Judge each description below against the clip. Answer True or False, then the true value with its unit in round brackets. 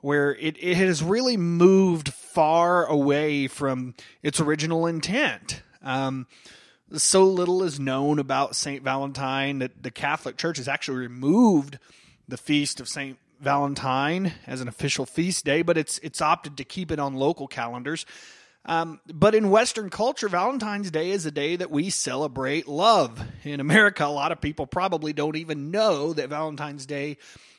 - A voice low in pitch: False (150 Hz)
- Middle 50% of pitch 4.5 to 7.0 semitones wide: False (4.1 semitones)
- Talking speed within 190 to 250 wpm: False (160 wpm)